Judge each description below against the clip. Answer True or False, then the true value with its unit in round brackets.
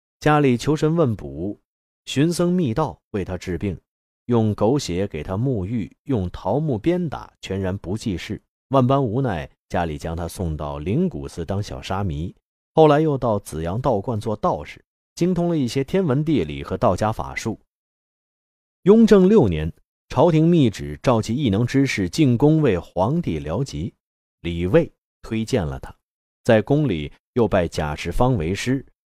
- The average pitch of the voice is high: False (110 Hz)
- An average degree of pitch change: False (8.5 semitones)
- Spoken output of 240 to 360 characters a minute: False (225 characters per minute)